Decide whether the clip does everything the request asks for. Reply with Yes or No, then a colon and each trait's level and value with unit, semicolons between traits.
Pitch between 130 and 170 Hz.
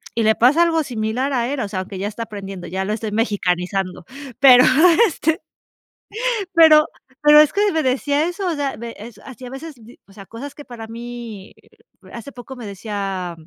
No: high, 235 Hz